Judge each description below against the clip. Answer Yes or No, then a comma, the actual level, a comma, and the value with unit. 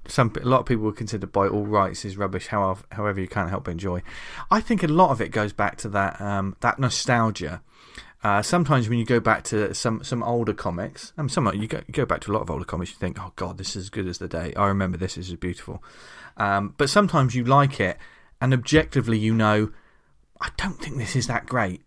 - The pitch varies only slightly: No, average, 4.2 semitones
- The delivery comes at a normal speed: No, fast, 250 wpm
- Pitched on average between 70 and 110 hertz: Yes, low, 105 Hz